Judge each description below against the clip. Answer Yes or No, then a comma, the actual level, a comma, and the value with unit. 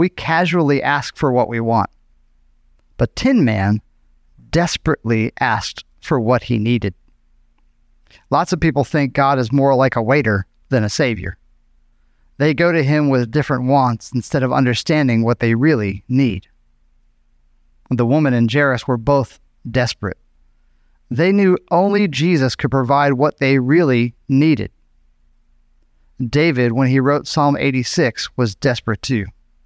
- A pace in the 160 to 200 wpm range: No, average, 140 wpm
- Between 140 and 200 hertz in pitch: No, low, 125 Hz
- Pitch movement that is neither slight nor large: No, wide, 7.1 semitones